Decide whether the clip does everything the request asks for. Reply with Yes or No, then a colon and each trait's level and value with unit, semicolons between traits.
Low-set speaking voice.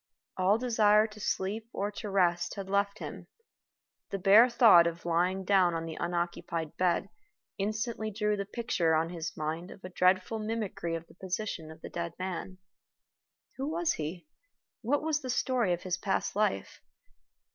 No: high, 190 Hz